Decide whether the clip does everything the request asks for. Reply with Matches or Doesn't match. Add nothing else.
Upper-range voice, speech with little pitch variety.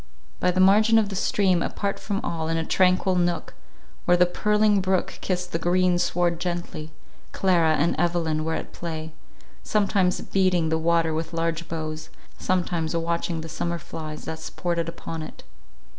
Doesn't match